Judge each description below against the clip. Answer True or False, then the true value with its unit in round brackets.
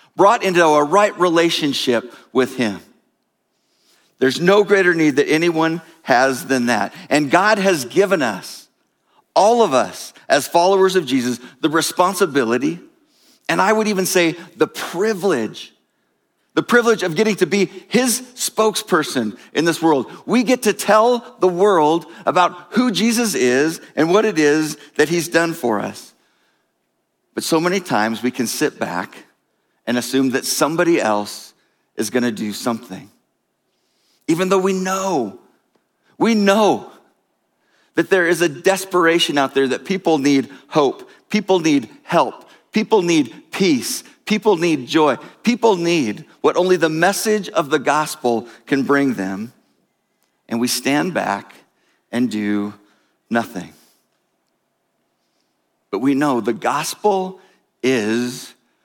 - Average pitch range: False (7.1 semitones)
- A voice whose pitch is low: False (170 Hz)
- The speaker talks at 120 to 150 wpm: True (140 wpm)